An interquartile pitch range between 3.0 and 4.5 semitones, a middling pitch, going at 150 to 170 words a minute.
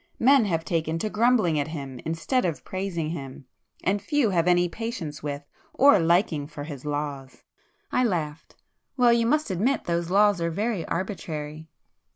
No: wide, 5.6 semitones; medium, 170 Hz; average, 160 wpm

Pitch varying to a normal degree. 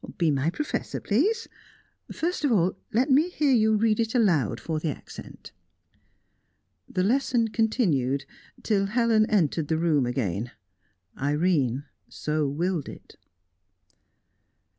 No: wide, 7.8 semitones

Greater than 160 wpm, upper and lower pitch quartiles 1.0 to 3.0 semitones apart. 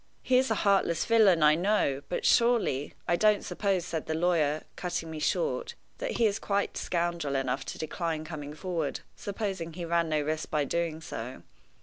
No: average, 190 wpm; average, 4.5 semitones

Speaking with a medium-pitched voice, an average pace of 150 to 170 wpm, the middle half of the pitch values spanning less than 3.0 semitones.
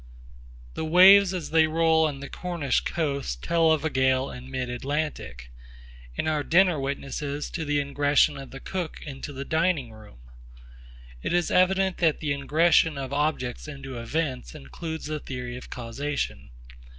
No: medium, 145 Hz; average, 165 wpm; average, 3.5 semitones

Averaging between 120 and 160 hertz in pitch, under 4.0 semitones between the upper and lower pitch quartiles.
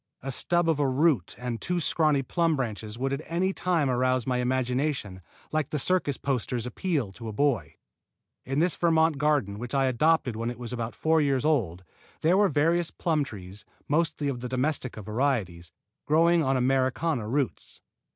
No: low, 135 Hz; average, 4.5 semitones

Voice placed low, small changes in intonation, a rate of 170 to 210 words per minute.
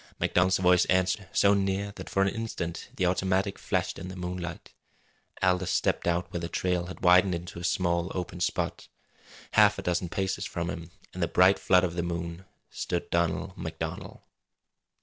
Yes: very low, 90 Hz; narrow, 1.4 semitones; average, 175 wpm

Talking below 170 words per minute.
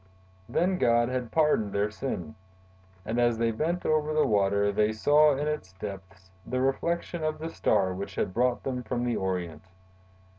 No: average, 175 wpm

